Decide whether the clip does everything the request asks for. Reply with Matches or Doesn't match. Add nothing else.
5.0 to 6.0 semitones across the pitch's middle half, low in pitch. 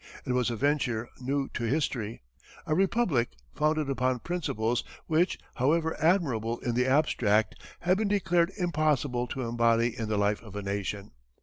Matches